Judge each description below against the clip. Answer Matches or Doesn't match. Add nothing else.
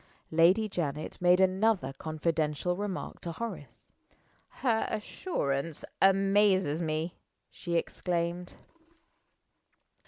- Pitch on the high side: Doesn't match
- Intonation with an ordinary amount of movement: Matches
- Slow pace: Matches